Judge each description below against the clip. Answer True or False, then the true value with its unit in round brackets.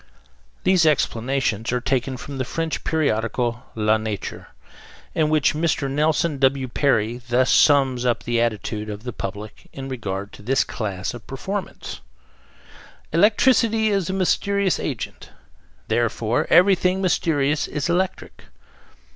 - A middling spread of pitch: False (6.0 semitones)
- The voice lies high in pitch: False (135 Hz)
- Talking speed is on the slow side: True (130 wpm)